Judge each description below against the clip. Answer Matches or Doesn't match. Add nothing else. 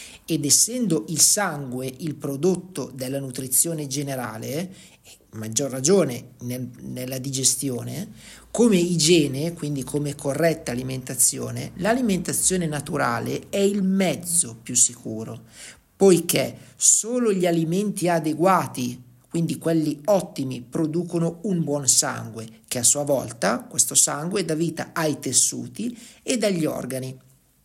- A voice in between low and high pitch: Matches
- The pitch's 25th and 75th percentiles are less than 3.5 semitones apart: Doesn't match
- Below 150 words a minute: Matches